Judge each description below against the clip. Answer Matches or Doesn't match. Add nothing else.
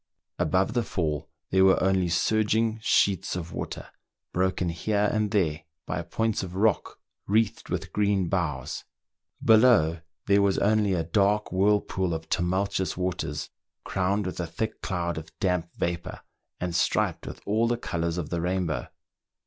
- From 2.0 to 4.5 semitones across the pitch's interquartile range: Matches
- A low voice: Matches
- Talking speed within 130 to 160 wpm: Matches